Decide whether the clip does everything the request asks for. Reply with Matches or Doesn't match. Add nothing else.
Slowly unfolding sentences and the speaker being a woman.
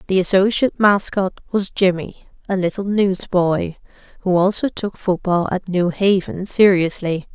Matches